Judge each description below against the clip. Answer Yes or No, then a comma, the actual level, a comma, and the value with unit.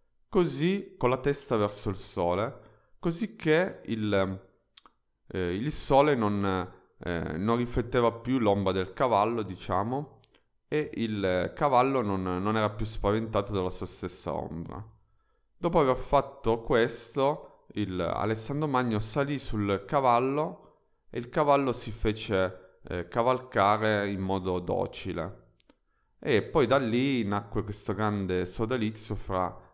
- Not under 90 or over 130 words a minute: Yes, average, 125 wpm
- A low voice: Yes, low, 110 Hz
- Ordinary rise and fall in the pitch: Yes, average, 4.8 semitones